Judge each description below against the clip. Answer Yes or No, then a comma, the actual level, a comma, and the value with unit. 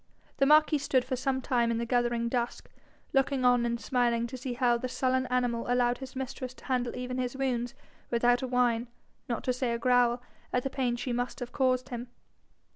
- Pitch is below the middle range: No, very high, 250 Hz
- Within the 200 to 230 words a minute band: Yes, fast, 205 wpm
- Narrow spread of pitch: Yes, narrow, 1.3 semitones